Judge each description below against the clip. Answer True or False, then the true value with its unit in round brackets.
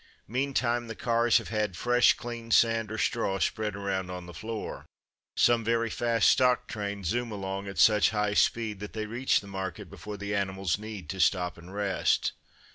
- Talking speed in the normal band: True (185 wpm)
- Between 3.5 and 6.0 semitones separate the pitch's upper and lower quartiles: False (3.0 semitones)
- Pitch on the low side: True (105 Hz)